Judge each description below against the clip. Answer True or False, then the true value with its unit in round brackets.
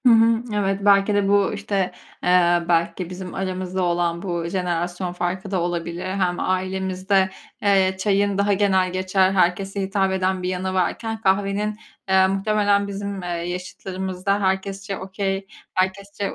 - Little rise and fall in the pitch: True (1.5 semitones)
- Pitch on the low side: False (190 Hz)